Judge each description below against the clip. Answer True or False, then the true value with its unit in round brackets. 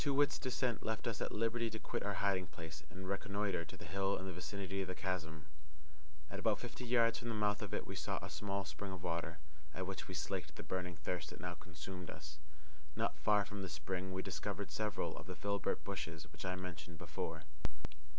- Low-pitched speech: True (95 Hz)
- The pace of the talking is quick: True (215 wpm)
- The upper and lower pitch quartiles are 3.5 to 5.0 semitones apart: False (2.8 semitones)